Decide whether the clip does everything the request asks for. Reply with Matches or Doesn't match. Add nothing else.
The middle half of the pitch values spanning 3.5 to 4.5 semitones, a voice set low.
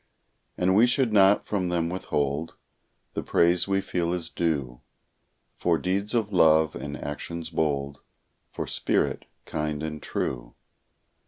Matches